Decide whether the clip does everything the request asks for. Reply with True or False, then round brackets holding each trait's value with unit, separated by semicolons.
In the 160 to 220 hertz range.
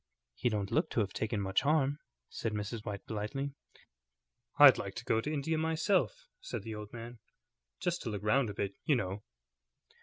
False (115 Hz)